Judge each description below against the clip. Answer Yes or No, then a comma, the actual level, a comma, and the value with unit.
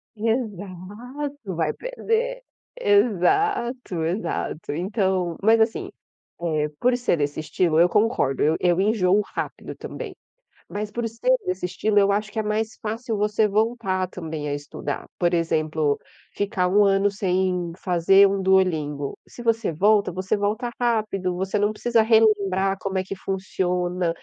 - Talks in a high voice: Yes, high, 195 Hz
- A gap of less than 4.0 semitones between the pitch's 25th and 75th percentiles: Yes, average, 3.6 semitones